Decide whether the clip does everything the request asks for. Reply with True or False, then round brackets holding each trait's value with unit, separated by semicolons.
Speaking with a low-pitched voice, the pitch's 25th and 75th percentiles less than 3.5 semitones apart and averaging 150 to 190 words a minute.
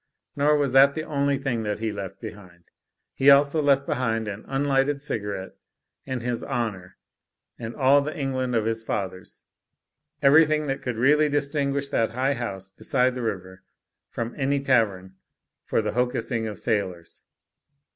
False (125 Hz; 4.6 semitones; 155 wpm)